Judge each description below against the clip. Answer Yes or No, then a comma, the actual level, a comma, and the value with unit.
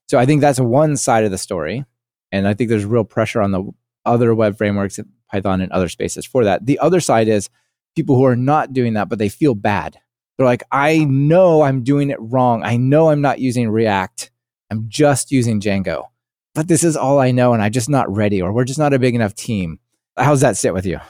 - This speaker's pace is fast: Yes, fast, 235 wpm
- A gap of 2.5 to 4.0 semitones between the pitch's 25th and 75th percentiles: No, average, 4.9 semitones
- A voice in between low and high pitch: No, low, 120 Hz